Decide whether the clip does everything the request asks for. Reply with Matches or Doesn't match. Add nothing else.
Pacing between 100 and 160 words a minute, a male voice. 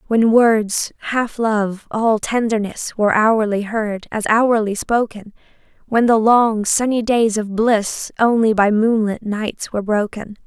Doesn't match